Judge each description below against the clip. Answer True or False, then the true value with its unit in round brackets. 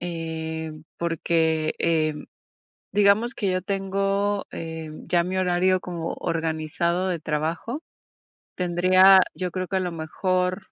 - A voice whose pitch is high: False (175 Hz)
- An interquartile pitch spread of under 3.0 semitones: True (2.6 semitones)